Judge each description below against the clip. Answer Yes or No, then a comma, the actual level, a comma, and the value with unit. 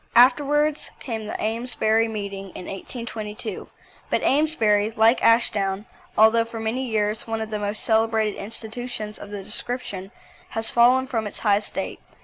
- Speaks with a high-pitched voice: Yes, high, 220 Hz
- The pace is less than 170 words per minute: Yes, average, 145 wpm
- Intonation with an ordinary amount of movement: No, narrow, 2.2 semitones